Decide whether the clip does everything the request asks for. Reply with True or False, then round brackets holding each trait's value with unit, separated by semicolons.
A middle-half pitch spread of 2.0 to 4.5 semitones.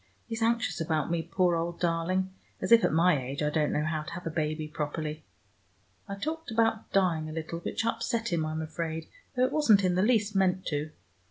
False (4.9 semitones)